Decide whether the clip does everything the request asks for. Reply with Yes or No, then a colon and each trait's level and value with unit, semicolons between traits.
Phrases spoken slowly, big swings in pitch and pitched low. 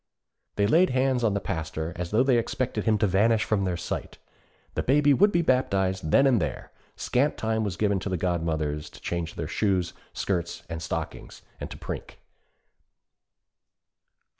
No: average, 170 wpm; wide, 6.3 semitones; low, 100 Hz